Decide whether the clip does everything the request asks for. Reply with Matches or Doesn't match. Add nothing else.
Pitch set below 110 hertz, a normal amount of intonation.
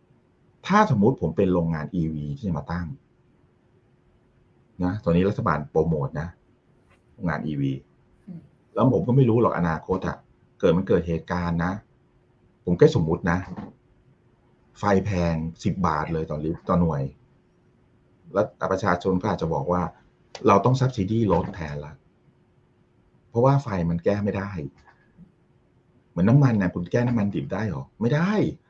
Matches